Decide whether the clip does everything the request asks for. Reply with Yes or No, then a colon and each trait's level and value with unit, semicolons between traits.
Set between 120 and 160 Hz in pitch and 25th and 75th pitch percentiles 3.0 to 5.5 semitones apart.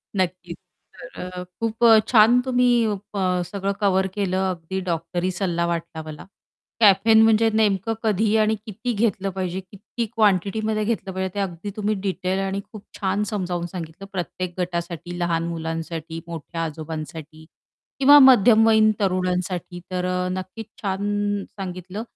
No: high, 190 Hz; average, 3.3 semitones